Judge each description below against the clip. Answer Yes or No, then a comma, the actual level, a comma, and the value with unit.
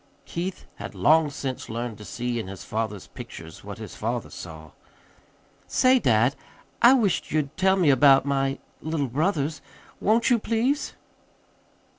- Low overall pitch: No, medium, 145 Hz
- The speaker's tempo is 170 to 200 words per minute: No, average, 145 wpm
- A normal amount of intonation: No, wide, 7.9 semitones